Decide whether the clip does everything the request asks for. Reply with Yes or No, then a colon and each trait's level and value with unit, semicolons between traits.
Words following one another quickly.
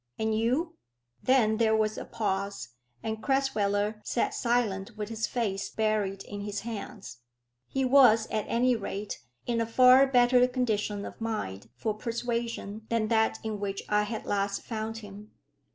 No: average, 155 wpm